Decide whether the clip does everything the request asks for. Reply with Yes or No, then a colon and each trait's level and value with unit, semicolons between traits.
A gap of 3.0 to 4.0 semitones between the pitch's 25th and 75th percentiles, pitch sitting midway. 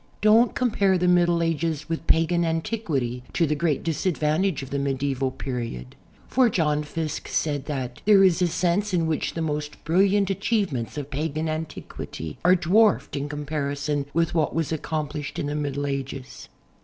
Yes: average, 3.6 semitones; medium, 155 Hz